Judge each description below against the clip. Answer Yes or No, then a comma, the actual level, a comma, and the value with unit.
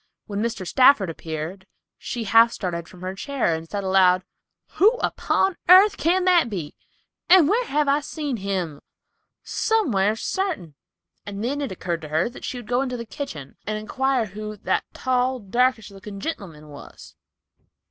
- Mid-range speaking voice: No, high, 215 Hz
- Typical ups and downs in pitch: No, wide, 6.9 semitones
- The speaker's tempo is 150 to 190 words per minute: Yes, average, 160 wpm